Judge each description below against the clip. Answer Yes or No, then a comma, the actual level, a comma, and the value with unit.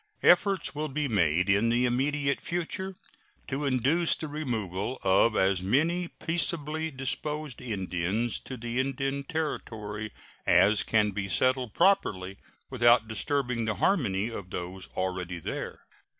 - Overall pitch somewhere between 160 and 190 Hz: No, low, 120 Hz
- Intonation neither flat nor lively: No, wide, 6.7 semitones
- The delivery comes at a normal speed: No, slow, 130 wpm